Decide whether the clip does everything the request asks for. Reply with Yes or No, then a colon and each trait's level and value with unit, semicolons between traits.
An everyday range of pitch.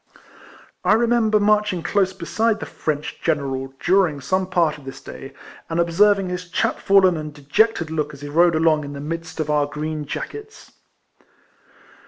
Yes: average, 4.6 semitones